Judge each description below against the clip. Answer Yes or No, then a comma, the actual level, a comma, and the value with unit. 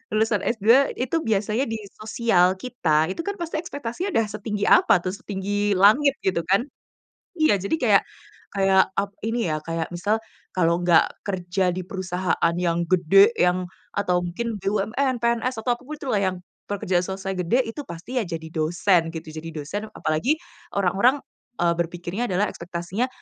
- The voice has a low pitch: No, high, 195 Hz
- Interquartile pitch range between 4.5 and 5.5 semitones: Yes, average, 4.8 semitones